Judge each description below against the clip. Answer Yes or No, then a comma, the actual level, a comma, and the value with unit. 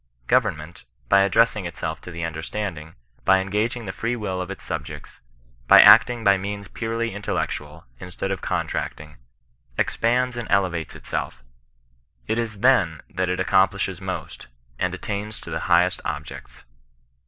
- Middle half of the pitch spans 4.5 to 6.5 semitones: No, average, 3.8 semitones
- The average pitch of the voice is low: Yes, very low, 95 Hz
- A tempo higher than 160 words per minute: No, average, 145 wpm